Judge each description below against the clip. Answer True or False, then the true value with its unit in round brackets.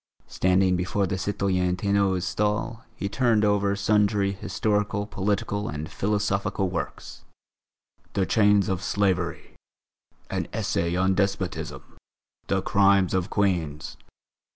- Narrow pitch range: True (1.8 semitones)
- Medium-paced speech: False (110 wpm)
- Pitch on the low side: True (100 Hz)